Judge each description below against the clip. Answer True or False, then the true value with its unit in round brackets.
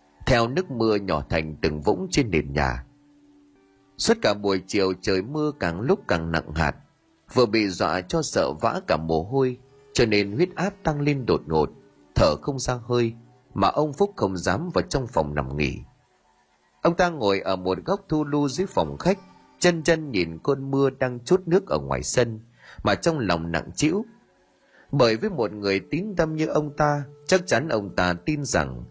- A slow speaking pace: False (195 wpm)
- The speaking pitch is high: False (115 Hz)